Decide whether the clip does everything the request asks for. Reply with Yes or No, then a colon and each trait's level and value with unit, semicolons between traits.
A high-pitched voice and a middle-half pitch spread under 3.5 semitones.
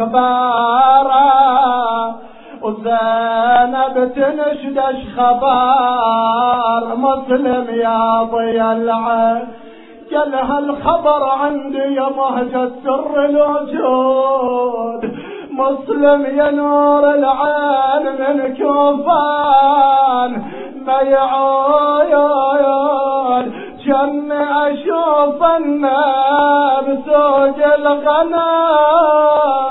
Yes: very high, 270 Hz; average, 2.7 semitones